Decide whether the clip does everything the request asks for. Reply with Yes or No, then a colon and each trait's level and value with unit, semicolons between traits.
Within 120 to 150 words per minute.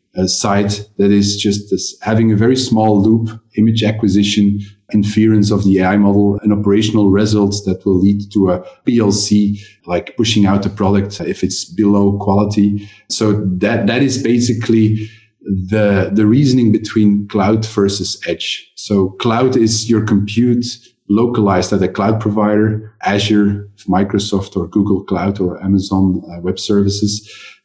Yes: average, 145 wpm